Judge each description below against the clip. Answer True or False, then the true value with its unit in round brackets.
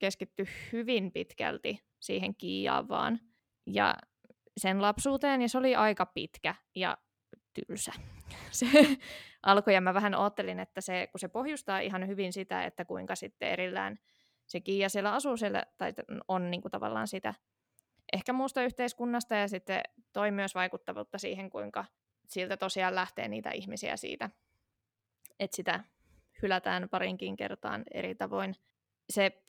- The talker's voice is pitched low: False (195 Hz)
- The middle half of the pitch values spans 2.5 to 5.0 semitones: True (4.5 semitones)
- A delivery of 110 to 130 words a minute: False (140 wpm)